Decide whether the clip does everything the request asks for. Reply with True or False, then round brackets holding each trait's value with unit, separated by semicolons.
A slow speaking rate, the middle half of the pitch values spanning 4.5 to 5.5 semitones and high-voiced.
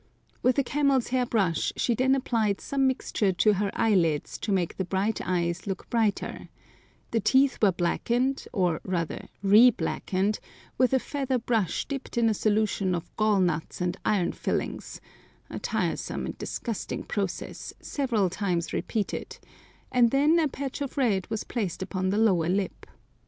False (155 wpm; 5.1 semitones; 215 Hz)